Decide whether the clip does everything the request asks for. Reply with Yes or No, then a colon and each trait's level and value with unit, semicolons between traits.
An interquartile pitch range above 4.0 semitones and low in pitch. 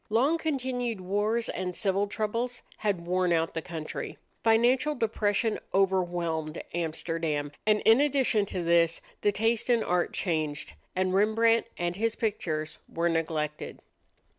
No: average, 5.1 semitones; high, 195 Hz